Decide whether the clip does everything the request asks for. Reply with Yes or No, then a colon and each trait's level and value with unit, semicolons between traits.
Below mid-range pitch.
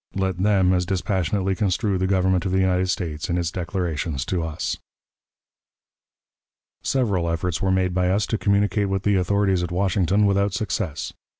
Yes: very low, 95 Hz